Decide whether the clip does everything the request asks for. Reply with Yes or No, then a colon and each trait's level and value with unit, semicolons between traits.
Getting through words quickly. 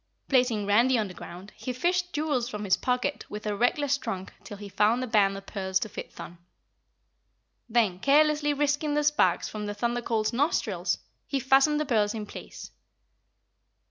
No: average, 175 wpm